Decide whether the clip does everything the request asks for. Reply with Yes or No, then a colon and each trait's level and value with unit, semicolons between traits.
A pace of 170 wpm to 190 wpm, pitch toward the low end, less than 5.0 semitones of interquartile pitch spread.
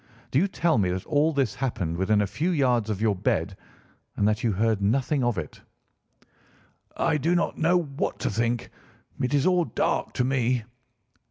No: average, 185 wpm; low, 125 Hz; wide, 5.4 semitones